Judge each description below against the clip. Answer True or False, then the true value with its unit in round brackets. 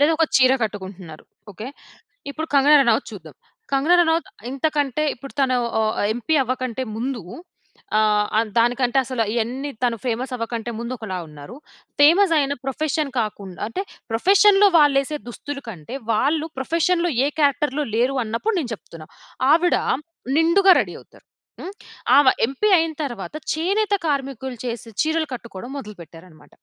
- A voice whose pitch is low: False (260 Hz)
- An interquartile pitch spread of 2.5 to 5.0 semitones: False (5.4 semitones)